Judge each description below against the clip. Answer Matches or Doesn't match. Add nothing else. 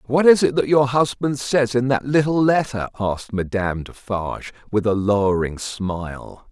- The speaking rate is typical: Matches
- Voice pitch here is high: Doesn't match